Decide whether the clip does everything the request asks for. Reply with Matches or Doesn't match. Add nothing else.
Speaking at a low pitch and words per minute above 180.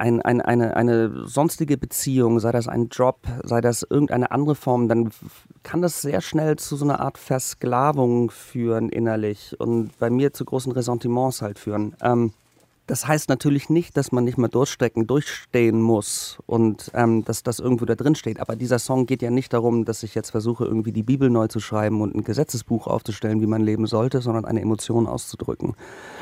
Matches